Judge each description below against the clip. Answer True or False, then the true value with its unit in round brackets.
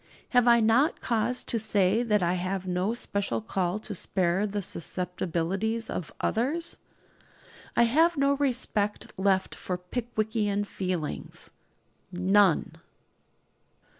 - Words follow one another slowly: True (115 wpm)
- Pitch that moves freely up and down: False (4.2 semitones)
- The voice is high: True (205 Hz)